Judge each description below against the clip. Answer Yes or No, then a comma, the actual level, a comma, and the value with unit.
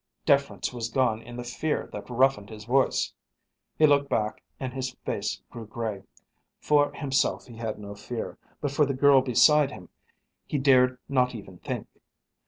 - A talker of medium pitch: No, low, 125 Hz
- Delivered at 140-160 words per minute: No, average, 170 wpm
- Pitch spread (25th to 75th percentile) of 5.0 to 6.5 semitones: No, average, 3.6 semitones